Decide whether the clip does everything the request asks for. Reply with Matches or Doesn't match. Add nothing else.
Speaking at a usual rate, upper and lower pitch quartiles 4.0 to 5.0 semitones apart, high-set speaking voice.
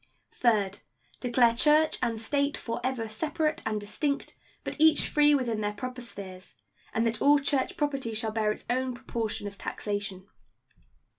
Matches